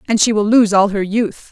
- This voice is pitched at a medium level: No, high, 210 Hz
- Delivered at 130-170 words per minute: No, fast, 275 wpm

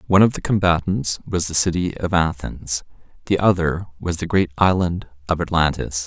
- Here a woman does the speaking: No, male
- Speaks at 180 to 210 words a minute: No, average, 170 wpm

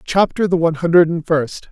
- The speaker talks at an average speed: No, fast, 210 wpm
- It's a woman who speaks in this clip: No, male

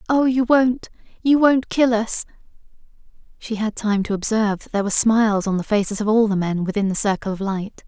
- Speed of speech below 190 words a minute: No, fast, 205 wpm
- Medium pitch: No, high, 220 Hz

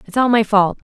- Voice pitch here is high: Yes, high, 215 Hz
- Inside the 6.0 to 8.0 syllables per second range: No, 5.7 syllables/s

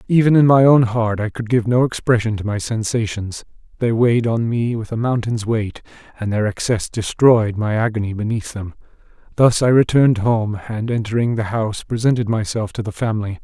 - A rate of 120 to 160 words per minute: No, average, 185 wpm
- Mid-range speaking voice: No, low, 115 Hz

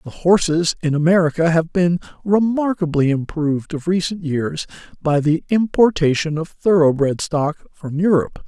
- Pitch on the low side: No, medium, 165 Hz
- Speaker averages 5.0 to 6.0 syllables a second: No, 4.7 syllables/s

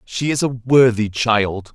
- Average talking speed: Yes, average, 170 wpm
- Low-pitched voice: Yes, low, 115 Hz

